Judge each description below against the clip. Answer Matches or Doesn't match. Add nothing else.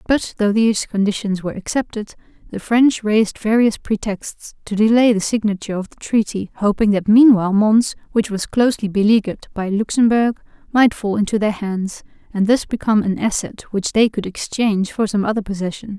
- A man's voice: Doesn't match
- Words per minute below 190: Matches